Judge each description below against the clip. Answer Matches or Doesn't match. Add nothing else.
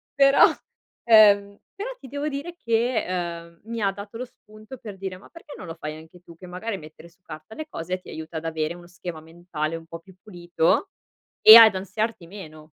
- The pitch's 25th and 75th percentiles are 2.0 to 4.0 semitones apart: Doesn't match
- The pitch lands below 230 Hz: Matches